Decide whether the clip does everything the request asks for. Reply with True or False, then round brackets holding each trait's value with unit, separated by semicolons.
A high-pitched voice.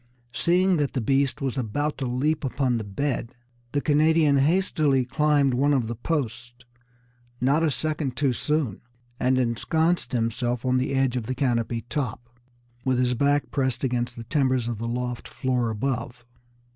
False (130 Hz)